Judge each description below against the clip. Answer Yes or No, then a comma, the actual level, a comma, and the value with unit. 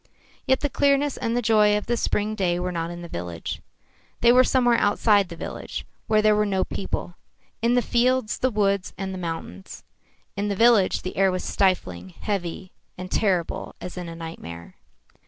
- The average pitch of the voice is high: Yes, high, 200 Hz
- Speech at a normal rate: Yes, average, 190 wpm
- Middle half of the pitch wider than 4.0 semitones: Yes, average, 4.6 semitones